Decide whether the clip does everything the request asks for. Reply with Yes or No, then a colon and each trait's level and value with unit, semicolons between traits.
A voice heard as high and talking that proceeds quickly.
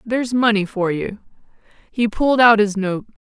No: high, 215 Hz; average, 165 wpm